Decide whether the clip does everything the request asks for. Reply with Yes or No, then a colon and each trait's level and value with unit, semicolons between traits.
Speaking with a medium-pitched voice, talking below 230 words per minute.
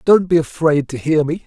No: medium, 155 Hz; fast, 245 wpm